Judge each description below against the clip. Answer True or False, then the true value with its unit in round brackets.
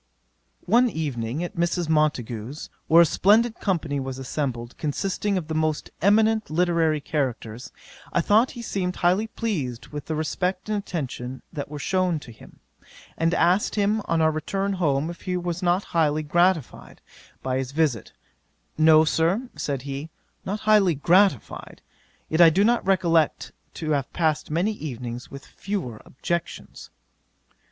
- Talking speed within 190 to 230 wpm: False (150 wpm)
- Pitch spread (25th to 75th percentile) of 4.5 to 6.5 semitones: True (4.8 semitones)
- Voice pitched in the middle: True (160 Hz)